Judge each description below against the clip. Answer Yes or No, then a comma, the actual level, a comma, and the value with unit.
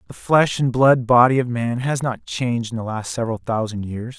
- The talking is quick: Yes, fast, 230 wpm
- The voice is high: No, low, 120 Hz